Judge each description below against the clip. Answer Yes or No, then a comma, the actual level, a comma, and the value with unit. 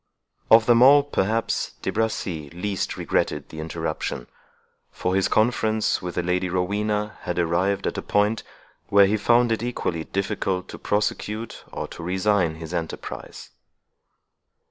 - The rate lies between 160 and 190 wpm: No, average, 145 wpm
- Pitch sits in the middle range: No, low, 100 Hz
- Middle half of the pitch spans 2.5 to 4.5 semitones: Yes, average, 3.6 semitones